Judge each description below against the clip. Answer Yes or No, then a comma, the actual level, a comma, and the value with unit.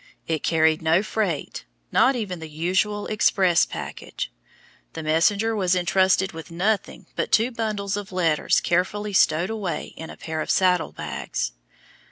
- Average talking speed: Yes, average, 150 wpm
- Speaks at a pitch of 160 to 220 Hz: Yes, medium, 185 Hz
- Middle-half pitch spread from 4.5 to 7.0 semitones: No, average, 4.1 semitones